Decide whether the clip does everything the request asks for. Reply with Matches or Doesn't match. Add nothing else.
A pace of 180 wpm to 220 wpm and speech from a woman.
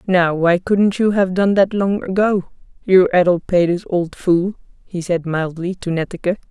Doesn't match